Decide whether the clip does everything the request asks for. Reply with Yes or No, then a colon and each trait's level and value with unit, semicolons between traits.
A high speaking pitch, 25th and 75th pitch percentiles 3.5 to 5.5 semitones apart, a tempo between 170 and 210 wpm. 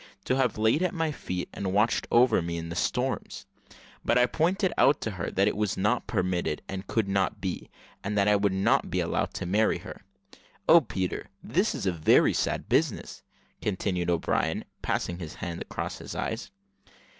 No: low, 100 Hz; average, 4.3 semitones; average, 190 wpm